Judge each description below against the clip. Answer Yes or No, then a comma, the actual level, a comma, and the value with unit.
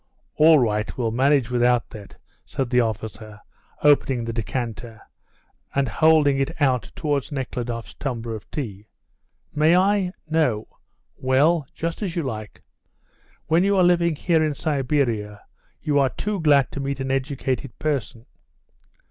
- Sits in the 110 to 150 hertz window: Yes, low, 135 Hz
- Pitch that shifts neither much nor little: Yes, average, 4.9 semitones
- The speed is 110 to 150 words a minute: Yes, average, 140 wpm